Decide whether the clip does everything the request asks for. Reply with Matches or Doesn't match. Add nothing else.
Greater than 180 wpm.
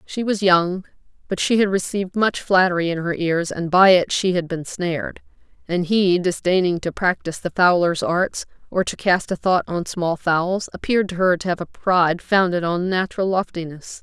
Matches